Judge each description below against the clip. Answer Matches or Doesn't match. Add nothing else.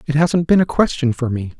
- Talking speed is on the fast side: Matches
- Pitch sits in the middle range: Matches